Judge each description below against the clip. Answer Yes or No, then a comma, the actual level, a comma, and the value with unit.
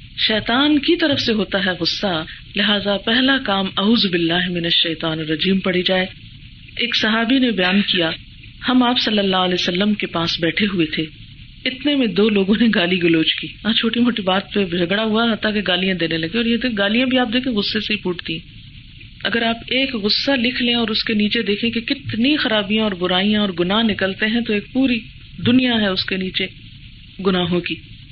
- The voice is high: Yes, high, 200 Hz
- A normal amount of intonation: Yes, average, 4.6 semitones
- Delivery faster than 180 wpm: Yes, fast, 190 wpm